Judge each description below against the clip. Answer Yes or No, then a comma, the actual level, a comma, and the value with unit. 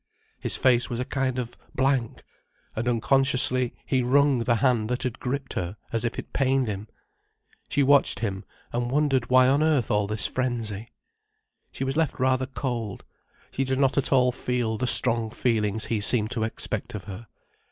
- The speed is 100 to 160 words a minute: No, average, 180 wpm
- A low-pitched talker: Yes, low, 125 Hz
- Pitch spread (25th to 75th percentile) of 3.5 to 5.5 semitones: No, average, 2.8 semitones